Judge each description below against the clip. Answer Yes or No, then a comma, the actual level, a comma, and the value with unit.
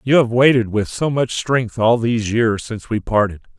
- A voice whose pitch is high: No, low, 115 Hz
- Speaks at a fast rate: Yes, fast, 215 wpm